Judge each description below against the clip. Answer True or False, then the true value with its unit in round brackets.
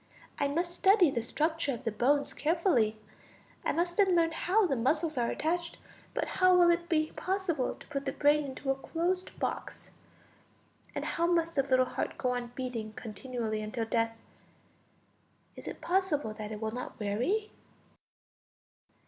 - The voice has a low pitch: False (285 Hz)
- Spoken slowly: False (160 wpm)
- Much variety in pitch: True (6.2 semitones)